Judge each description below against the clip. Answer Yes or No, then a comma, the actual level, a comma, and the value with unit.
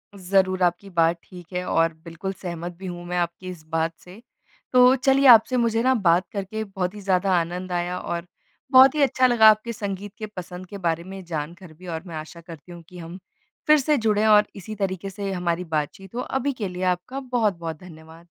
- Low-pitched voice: No, medium, 185 Hz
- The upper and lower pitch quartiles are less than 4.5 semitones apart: Yes, average, 3.9 semitones